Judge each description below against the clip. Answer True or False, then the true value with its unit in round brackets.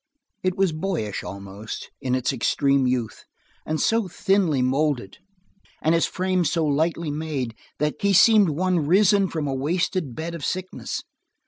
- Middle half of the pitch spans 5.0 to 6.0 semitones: True (5.5 semitones)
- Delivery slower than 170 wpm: True (150 wpm)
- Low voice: False (155 Hz)